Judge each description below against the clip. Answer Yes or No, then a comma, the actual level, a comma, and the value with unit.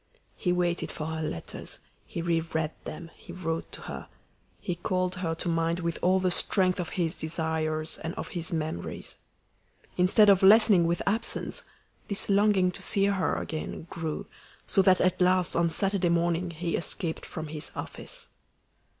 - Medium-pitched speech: Yes, medium, 175 Hz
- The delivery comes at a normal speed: Yes, average, 165 wpm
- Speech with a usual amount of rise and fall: No, narrow, 2.2 semitones